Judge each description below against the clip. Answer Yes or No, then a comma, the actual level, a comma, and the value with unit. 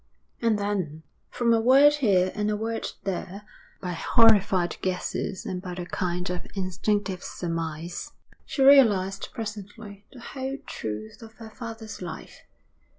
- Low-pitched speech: No, high, 200 Hz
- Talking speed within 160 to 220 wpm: No, average, 140 wpm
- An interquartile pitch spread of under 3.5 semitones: No, average, 3.8 semitones